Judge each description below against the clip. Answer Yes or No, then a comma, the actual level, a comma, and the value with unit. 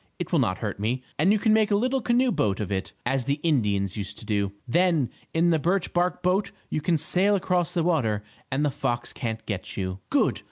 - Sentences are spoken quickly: Yes, fast, 230 wpm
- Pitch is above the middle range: No, medium, 150 Hz